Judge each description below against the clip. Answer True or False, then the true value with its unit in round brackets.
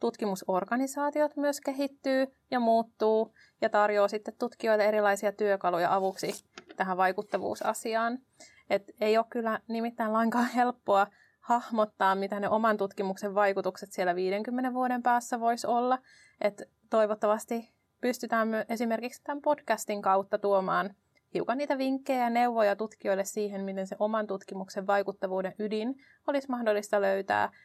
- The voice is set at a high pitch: True (220 Hz)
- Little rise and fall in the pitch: False (3.4 semitones)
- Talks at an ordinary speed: True (125 wpm)